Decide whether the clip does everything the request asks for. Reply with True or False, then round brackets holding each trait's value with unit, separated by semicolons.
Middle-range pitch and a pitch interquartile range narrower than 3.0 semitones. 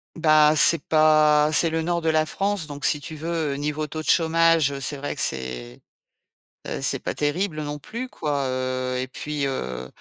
True (150 Hz; 2.6 semitones)